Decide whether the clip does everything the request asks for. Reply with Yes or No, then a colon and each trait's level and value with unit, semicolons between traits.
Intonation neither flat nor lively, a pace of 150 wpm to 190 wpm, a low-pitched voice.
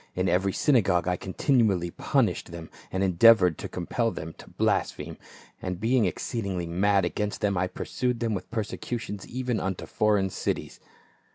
Yes: average, 3.9 semitones; average, 155 wpm; low, 100 Hz